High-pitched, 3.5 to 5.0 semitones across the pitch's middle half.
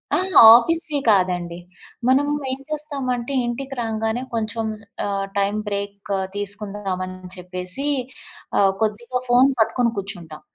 Yes: high, 215 Hz; average, 4.4 semitones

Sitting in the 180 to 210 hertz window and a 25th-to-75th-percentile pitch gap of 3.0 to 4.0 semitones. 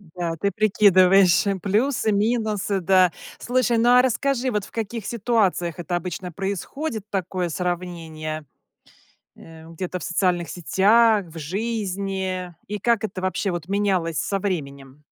Yes: high, 190 Hz; average, 3.6 semitones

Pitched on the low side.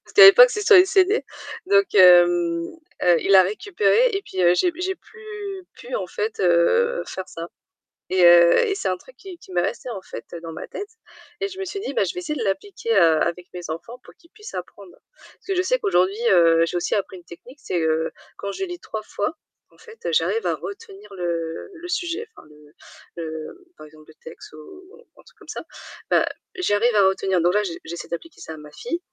No: high, 230 Hz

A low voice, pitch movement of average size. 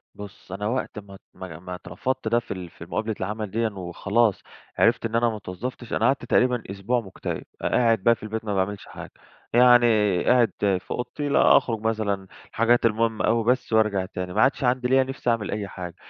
Yes: low, 110 Hz; average, 3.5 semitones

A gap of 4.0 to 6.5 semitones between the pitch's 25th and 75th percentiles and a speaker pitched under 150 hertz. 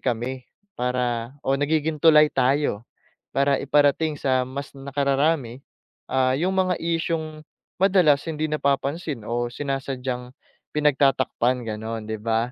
No: average, 3.3 semitones; low, 135 Hz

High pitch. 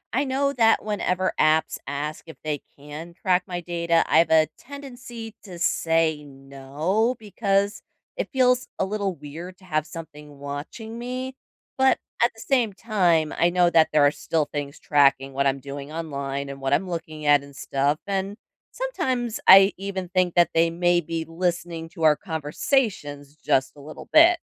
No: medium, 170 Hz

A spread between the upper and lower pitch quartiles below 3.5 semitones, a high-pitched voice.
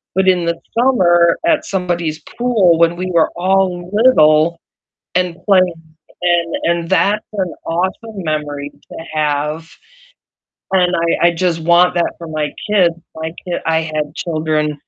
No: narrow, 2.6 semitones; medium, 170 Hz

